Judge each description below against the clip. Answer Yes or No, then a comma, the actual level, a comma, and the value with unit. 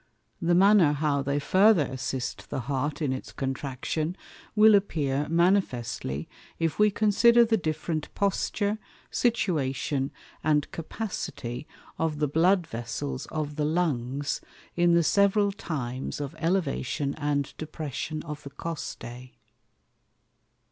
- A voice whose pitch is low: No, medium, 155 Hz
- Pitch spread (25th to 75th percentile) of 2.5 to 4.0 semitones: No, average, 4.9 semitones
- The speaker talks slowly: Yes, slow, 120 wpm